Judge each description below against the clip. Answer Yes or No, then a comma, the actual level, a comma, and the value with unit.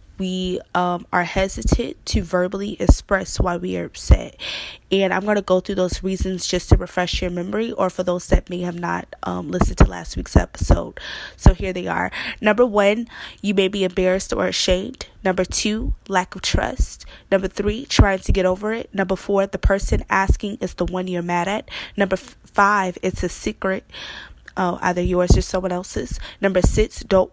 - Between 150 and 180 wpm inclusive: No, average, 190 wpm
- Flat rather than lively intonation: Yes, narrow, 1.9 semitones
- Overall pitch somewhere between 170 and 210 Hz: Yes, high, 190 Hz